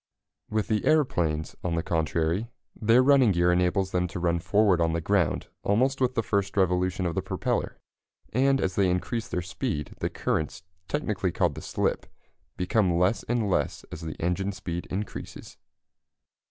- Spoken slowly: No, average, 165 wpm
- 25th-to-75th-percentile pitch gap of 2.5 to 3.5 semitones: No, average, 4.1 semitones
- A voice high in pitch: No, very low, 95 Hz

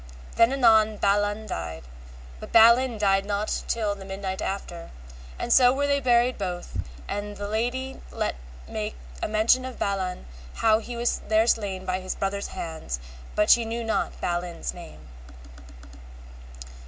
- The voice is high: Yes, high, 210 Hz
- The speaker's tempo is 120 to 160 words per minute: Yes, average, 150 wpm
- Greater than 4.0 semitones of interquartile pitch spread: No, average, 3.5 semitones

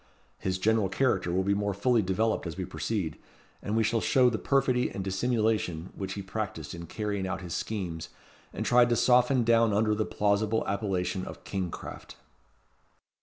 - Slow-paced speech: No, average, 175 wpm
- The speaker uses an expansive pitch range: No, average, 3.3 semitones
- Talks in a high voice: No, low, 105 Hz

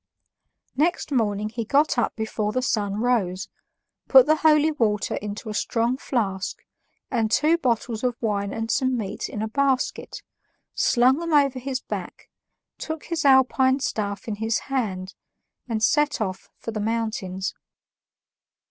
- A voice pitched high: Yes, high, 230 Hz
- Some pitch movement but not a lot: Yes, average, 4.2 semitones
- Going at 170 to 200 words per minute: No, average, 150 wpm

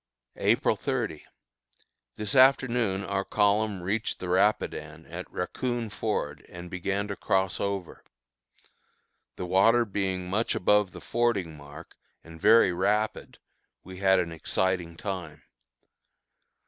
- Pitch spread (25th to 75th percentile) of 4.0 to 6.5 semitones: No, average, 3.1 semitones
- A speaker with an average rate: No, slow, 120 wpm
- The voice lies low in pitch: Yes, very low, 95 Hz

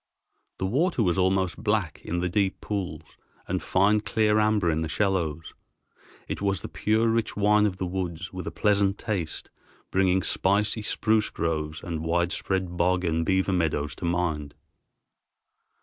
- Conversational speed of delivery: Yes, average, 155 wpm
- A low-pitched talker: Yes, very low, 95 Hz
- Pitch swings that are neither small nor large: Yes, average, 3.5 semitones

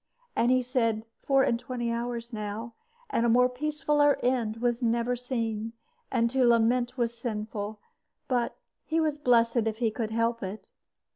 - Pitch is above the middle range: Yes, high, 235 Hz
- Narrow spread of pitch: Yes, narrow, 1.8 semitones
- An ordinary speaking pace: Yes, average, 160 wpm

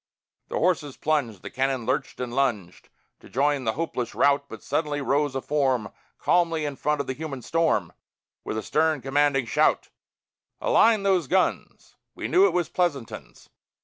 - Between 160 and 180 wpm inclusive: Yes, average, 165 wpm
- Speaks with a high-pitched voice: No, medium, 140 Hz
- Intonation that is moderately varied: Yes, average, 3.7 semitones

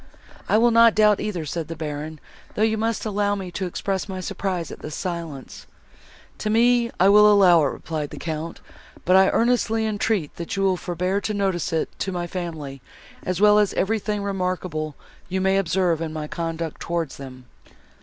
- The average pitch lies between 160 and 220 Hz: Yes, medium, 185 Hz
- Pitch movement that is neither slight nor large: Yes, average, 4.1 semitones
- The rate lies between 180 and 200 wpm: Yes, average, 185 wpm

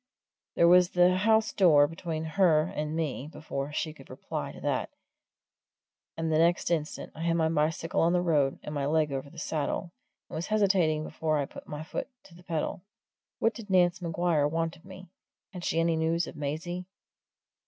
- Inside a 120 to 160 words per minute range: No, average, 190 wpm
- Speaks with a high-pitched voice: No, medium, 165 Hz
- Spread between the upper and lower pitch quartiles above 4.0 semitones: No, narrow, 2.5 semitones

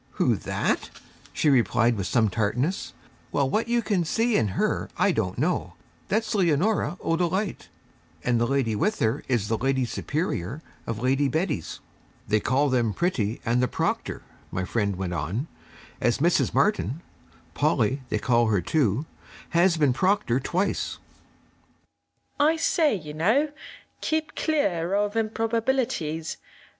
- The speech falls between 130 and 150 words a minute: Yes, average, 140 wpm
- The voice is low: No, medium, 150 Hz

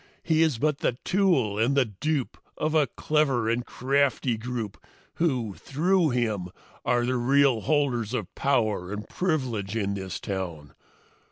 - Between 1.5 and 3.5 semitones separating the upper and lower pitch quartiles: No, average, 5.0 semitones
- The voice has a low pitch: Yes, low, 125 Hz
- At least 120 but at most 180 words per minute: Yes, average, 150 wpm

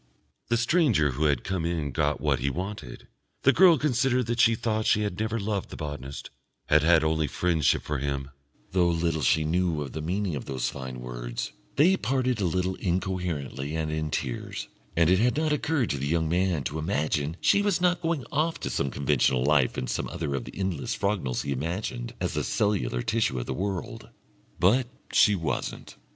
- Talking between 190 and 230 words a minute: Yes, average, 195 wpm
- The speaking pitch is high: No, very low, 85 Hz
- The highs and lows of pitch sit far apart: Yes, wide, 7.0 semitones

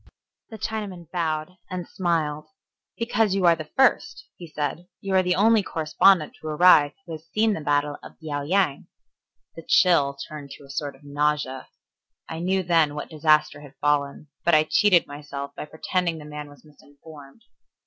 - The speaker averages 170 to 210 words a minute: Yes, average, 175 wpm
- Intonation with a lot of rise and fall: No, average, 3.7 semitones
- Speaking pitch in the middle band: Yes, medium, 155 Hz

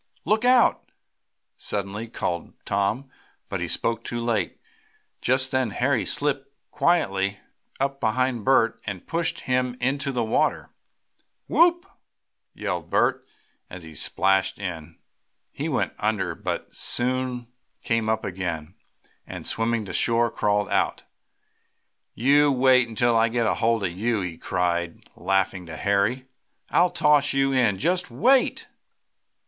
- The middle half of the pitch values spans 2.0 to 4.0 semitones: No, average, 5.2 semitones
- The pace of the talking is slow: Yes, slow, 130 wpm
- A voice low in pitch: Yes, low, 115 Hz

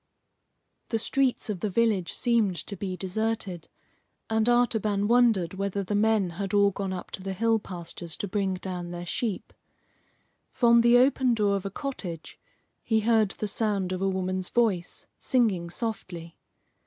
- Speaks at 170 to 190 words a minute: No, average, 160 wpm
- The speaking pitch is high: Yes, high, 200 Hz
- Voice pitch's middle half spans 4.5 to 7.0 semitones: No, average, 3.4 semitones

